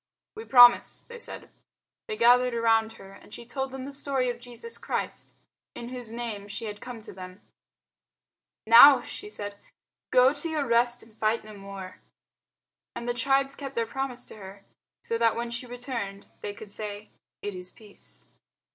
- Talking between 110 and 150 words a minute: No, average, 175 wpm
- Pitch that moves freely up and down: No, average, 3.4 semitones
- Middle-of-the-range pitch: No, high, 235 Hz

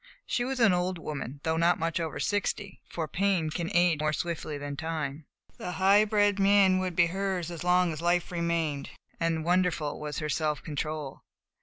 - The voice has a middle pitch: Yes, medium, 170 Hz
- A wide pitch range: No, average, 3.2 semitones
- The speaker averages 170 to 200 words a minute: Yes, average, 185 wpm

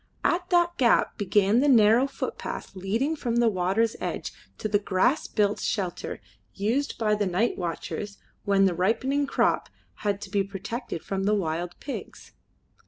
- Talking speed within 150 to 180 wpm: Yes, average, 160 wpm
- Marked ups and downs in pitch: No, average, 3.8 semitones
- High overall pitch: Yes, high, 210 Hz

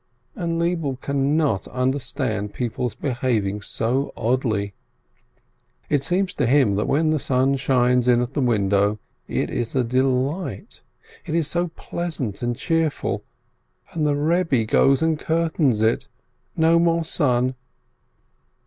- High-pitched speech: No, low, 135 Hz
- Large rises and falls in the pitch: No, average, 4.7 semitones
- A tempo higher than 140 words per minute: No, slow, 135 wpm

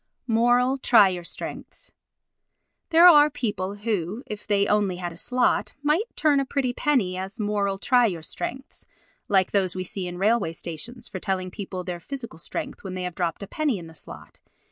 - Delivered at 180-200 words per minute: Yes, average, 190 wpm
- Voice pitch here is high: Yes, high, 205 Hz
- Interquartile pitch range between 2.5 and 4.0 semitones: No, average, 5.2 semitones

